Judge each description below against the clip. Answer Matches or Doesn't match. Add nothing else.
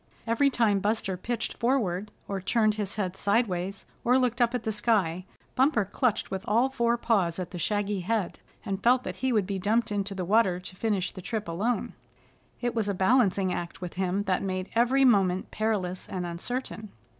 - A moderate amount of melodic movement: Matches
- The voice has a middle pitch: Doesn't match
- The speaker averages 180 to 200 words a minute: Matches